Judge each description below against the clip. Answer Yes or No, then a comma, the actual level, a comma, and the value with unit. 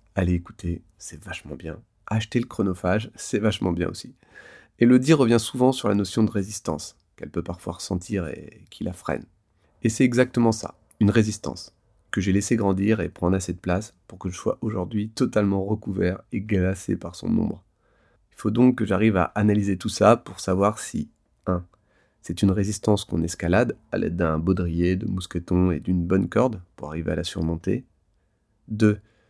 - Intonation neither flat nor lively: Yes, average, 3.6 semitones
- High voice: No, very low, 95 Hz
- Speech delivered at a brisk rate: No, average, 190 wpm